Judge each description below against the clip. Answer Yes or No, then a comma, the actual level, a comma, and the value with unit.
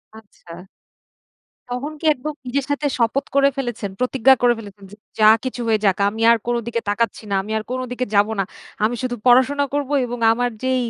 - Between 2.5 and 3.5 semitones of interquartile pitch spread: Yes, average, 2.9 semitones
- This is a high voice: Yes, high, 245 Hz